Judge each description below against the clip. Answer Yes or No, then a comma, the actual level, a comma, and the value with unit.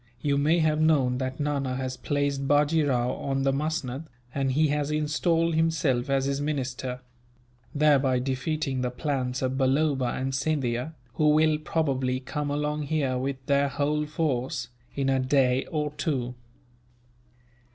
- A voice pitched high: No, medium, 140 Hz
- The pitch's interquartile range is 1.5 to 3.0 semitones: Yes, narrow, 2.6 semitones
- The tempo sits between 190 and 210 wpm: No, average, 150 wpm